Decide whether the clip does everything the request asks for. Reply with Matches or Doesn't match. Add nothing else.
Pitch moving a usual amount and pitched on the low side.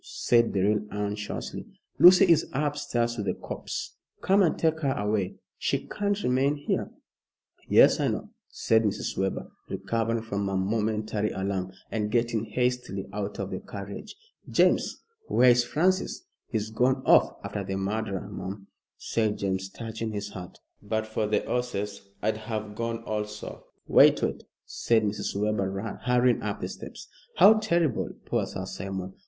Matches